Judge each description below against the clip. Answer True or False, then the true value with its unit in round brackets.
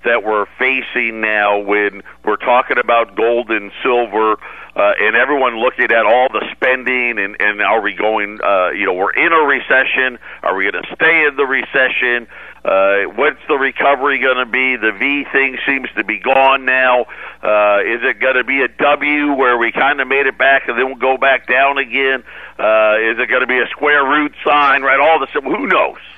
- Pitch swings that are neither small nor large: True (3.7 semitones)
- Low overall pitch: True (125 Hz)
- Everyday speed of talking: False (210 wpm)